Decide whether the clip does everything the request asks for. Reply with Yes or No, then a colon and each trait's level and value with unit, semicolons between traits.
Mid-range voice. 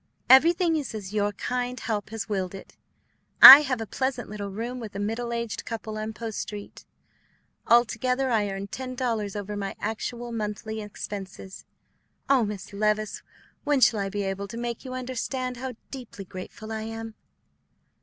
No: high, 220 Hz